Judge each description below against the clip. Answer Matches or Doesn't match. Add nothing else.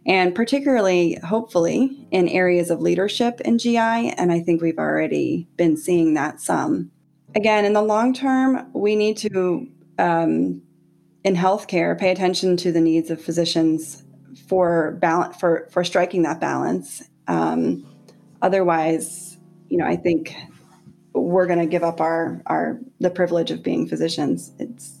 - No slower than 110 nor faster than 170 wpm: Matches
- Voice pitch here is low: Doesn't match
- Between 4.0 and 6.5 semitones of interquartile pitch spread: Doesn't match